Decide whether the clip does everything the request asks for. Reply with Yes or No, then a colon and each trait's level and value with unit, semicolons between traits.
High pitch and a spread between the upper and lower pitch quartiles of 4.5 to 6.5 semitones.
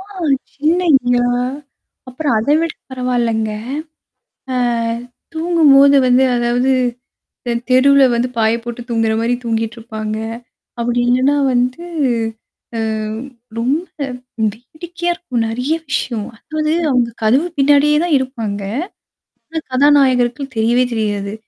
No: very high, 250 Hz; average, 3.7 semitones